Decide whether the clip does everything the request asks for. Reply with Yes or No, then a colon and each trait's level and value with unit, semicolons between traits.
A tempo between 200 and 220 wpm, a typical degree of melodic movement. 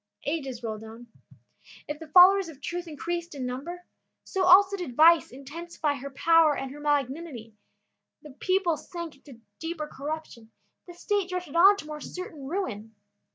No: average, 155 wpm; average, 4.4 semitones